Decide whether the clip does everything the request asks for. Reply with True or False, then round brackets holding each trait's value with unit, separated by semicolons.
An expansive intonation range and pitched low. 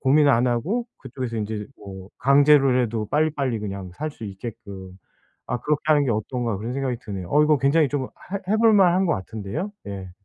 True (6.0 semitones; 125 Hz)